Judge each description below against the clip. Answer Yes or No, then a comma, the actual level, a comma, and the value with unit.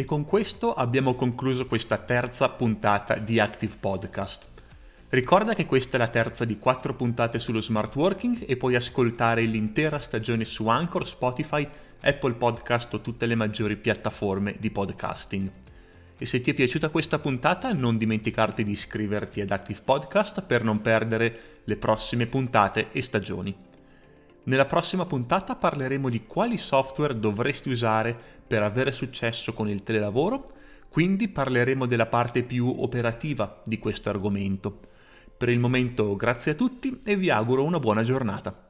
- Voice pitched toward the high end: No, low, 120 Hz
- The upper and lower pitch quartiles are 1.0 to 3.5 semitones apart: No, average, 3.9 semitones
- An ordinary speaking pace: Yes, average, 150 wpm